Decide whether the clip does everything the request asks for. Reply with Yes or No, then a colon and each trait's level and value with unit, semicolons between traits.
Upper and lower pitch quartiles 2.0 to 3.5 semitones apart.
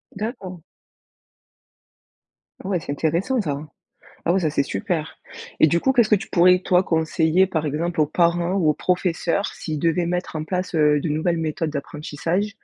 Yes: average, 2.8 semitones